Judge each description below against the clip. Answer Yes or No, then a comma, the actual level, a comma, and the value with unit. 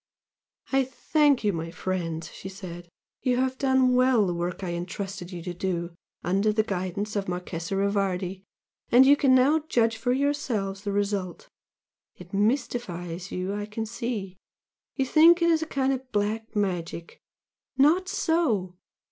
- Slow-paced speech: No, average, 160 wpm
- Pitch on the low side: No, high, 205 Hz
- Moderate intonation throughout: No, wide, 6.1 semitones